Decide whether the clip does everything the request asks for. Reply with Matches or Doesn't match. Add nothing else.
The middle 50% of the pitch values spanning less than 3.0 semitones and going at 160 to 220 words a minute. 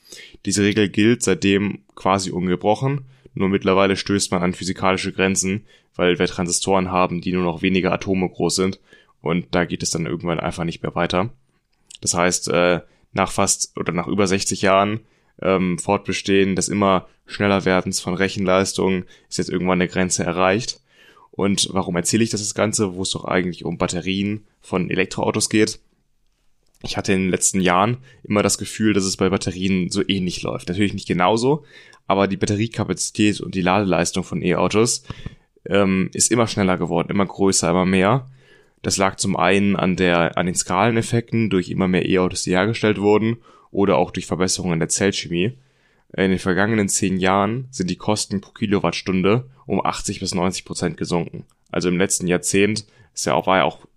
Matches